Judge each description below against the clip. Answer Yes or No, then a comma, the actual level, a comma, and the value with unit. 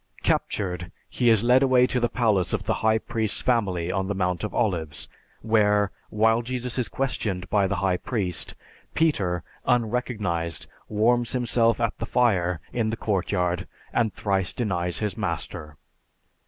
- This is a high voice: No, low, 105 Hz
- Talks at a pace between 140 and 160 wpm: Yes, average, 155 wpm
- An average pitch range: Yes, average, 4.8 semitones